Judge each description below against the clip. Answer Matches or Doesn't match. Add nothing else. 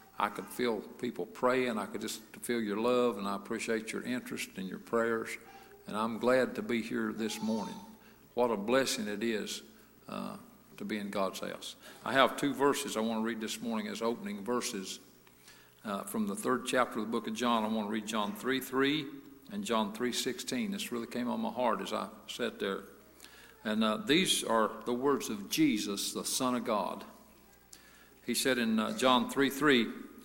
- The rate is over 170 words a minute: Matches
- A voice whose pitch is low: Matches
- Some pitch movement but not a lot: Matches